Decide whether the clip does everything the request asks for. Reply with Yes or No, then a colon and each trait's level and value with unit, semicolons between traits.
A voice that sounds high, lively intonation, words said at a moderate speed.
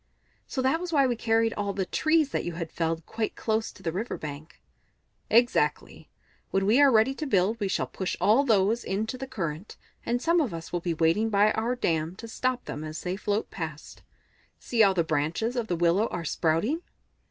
No: high, 210 Hz; wide, 6.0 semitones; fast, 210 wpm